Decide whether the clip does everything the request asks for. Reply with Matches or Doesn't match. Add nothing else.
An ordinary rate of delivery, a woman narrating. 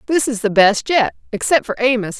Matches